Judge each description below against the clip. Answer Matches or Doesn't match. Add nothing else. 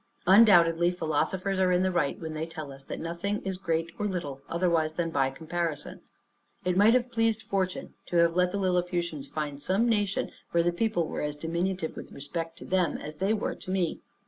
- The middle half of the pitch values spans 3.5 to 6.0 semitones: Doesn't match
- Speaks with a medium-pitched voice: Matches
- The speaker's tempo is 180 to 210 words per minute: Matches